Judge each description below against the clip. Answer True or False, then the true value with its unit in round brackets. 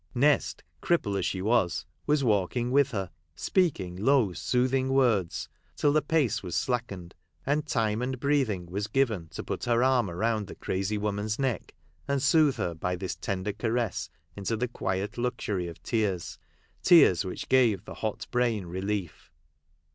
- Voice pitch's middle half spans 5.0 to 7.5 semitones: True (5.3 semitones)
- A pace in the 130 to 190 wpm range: True (160 wpm)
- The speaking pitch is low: True (110 Hz)